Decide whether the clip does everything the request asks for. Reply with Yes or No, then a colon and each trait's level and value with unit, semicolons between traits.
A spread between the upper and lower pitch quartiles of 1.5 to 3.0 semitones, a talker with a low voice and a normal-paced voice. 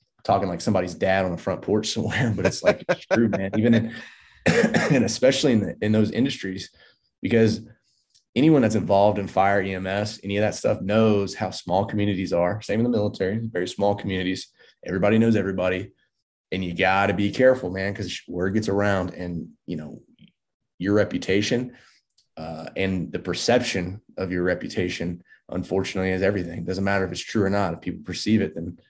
Yes: narrow, 2.4 semitones; low, 100 Hz; average, 185 wpm